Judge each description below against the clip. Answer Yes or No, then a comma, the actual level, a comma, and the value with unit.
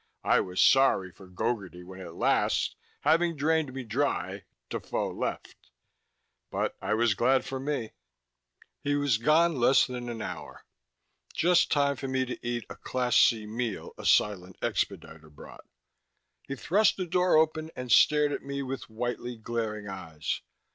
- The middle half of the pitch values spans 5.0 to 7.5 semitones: Yes, average, 5.3 semitones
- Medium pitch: No, low, 125 Hz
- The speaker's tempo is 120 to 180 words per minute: Yes, average, 155 wpm